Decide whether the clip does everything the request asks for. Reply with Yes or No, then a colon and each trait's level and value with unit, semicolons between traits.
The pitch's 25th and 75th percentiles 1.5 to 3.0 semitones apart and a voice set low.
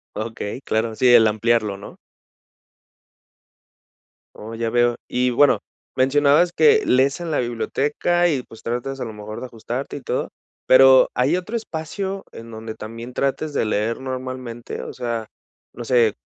No: average, 3.5 semitones; low, 125 Hz